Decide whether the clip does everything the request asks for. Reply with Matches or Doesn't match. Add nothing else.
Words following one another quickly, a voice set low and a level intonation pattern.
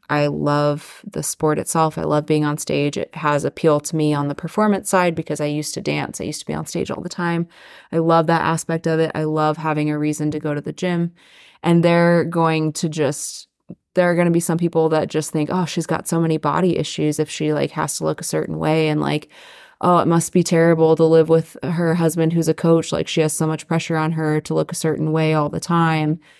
Doesn't match